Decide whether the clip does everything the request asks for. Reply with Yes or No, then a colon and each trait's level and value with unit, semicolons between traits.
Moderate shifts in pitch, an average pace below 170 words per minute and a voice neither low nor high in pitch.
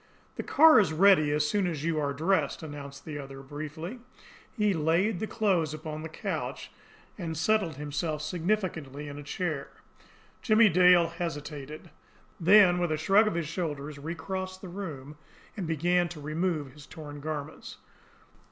Yes: average, 3.6 semitones; average, 155 wpm; medium, 160 Hz